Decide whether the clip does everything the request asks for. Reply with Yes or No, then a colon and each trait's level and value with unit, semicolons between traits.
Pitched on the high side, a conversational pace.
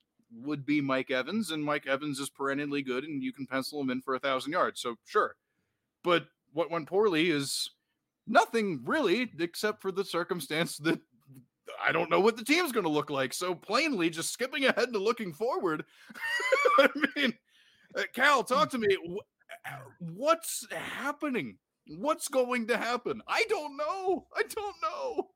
Yes: high, 200 Hz; average, 165 wpm